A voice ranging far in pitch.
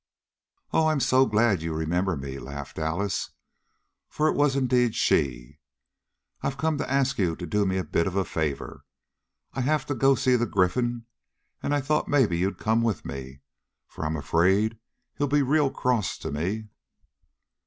Yes: wide, 8.3 semitones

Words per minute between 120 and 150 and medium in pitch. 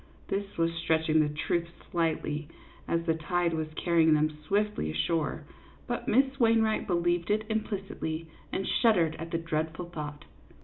Yes: average, 145 wpm; medium, 165 Hz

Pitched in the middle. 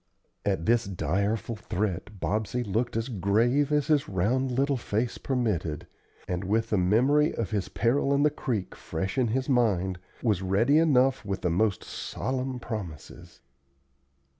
No: low, 110 Hz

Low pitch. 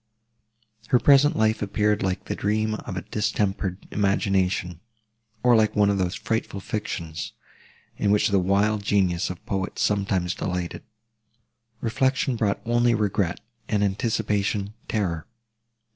Yes: low, 100 Hz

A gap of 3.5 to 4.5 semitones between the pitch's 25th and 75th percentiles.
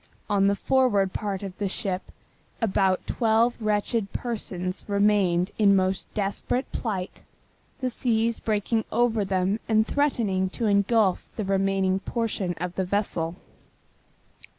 No: average, 2.8 semitones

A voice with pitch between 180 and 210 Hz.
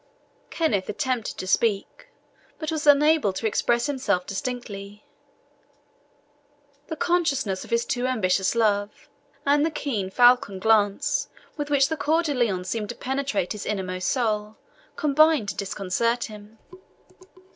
No: high, 235 Hz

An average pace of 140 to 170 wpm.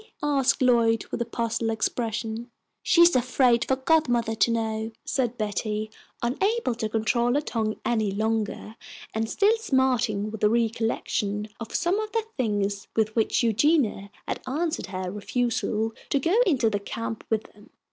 Yes: average, 155 wpm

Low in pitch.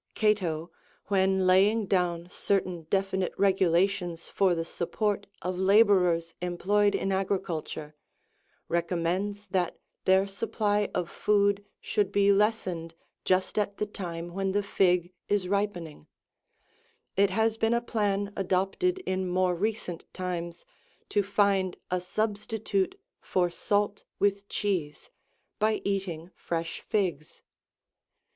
No: high, 190 Hz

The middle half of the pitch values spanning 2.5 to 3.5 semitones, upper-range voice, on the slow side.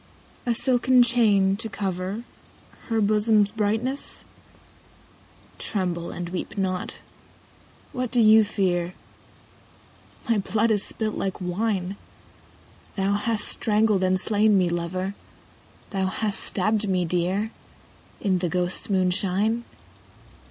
Yes: average, 3.0 semitones; high, 200 Hz; slow, 115 wpm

